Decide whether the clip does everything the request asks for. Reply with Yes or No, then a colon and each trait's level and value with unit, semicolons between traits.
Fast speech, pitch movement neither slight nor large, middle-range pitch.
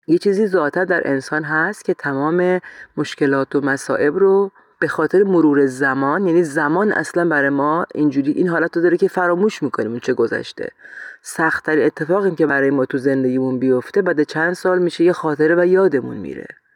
Yes: fast, 175 wpm; average, 4.6 semitones; medium, 165 Hz